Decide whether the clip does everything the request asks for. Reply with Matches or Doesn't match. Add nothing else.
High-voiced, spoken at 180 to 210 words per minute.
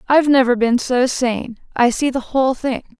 Matches